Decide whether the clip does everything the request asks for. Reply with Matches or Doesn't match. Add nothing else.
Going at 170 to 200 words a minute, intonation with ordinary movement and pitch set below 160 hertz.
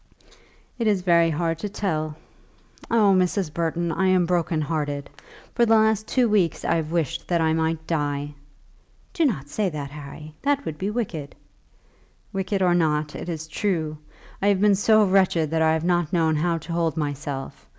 Doesn't match